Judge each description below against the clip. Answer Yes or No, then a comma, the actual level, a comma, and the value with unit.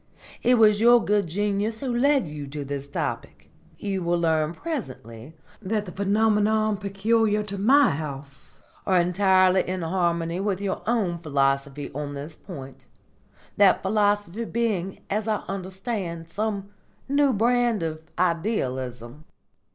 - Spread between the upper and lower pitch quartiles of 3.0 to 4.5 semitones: No, average, 5.1 semitones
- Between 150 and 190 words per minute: No, slow, 135 wpm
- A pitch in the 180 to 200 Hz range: Yes, high, 190 Hz